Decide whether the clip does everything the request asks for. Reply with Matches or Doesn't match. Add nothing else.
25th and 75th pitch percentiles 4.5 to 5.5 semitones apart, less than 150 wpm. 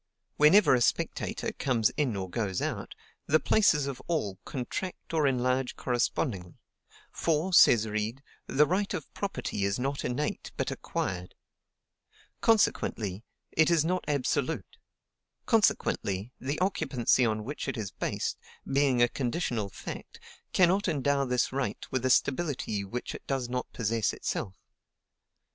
Matches